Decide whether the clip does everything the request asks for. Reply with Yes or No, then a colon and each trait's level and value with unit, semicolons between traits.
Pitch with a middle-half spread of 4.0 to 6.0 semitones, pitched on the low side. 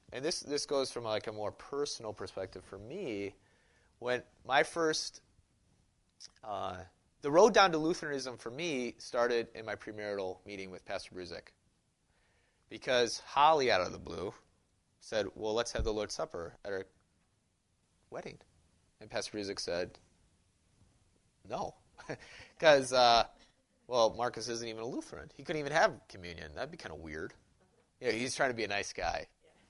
Yes: average, 4.8 semitones; low, 110 Hz